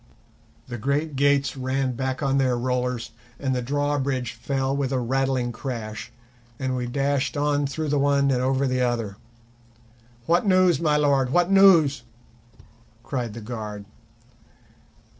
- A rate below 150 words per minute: Yes, average, 140 wpm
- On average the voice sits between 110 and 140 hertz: Yes, low, 135 Hz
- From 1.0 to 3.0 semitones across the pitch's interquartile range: Yes, narrow, 2.4 semitones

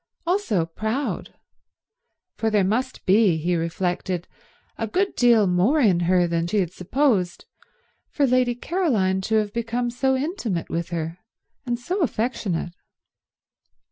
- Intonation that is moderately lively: No, wide, 6.0 semitones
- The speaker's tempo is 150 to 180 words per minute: No, slow, 135 wpm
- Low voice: No, high, 215 Hz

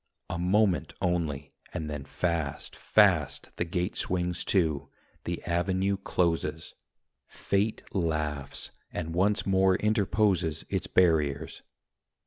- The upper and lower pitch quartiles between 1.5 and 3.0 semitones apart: No, average, 3.5 semitones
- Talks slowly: Yes, slow, 110 wpm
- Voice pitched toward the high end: No, very low, 85 Hz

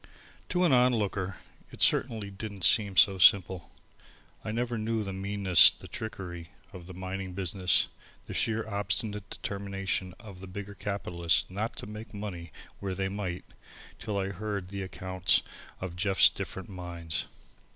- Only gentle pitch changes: Yes, narrow, 2.1 semitones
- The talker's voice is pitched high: No, very low, 95 Hz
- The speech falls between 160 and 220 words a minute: No, average, 150 wpm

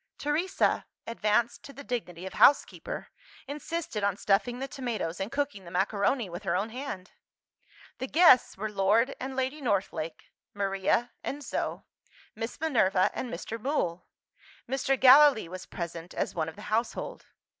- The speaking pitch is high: Yes, high, 225 Hz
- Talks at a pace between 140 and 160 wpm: Yes, average, 150 wpm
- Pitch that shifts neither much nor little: No, wide, 6.0 semitones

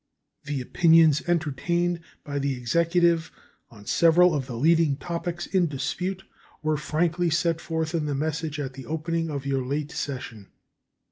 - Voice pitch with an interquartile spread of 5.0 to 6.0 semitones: No, average, 3.2 semitones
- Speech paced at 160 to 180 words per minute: No, average, 150 wpm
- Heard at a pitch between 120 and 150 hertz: No, medium, 160 Hz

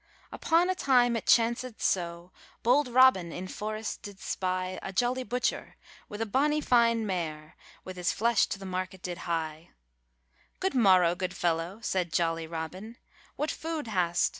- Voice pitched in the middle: No, high, 195 Hz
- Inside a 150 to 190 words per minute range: Yes, average, 160 wpm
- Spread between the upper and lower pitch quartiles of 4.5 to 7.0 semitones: Yes, wide, 5.5 semitones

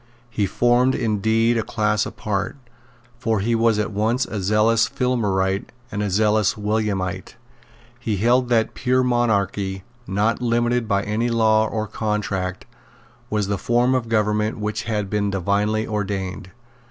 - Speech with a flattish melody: Yes, narrow, 2.3 semitones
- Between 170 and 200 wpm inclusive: No, average, 140 wpm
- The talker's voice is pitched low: Yes, low, 110 Hz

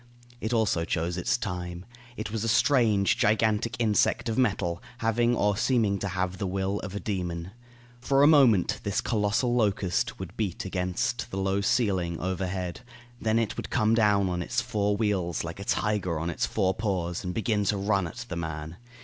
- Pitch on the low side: Yes, low, 100 Hz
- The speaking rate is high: No, average, 185 wpm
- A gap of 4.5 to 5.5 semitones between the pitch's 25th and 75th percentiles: No, average, 3.5 semitones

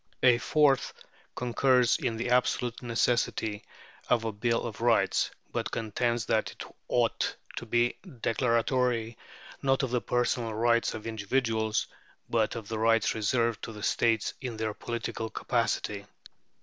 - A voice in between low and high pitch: No, low, 115 Hz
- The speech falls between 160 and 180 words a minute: No, average, 140 wpm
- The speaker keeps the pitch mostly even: Yes, narrow, 1.7 semitones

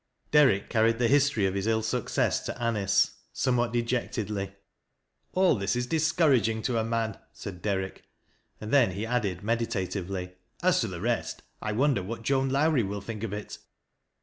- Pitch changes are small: No, average, 3.6 semitones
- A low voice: Yes, low, 115 Hz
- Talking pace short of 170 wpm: No, average, 175 wpm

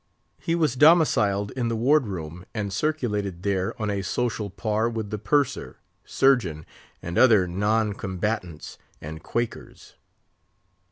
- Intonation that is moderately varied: Yes, average, 4.2 semitones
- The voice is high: No, low, 105 Hz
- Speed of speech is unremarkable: No, slow, 130 wpm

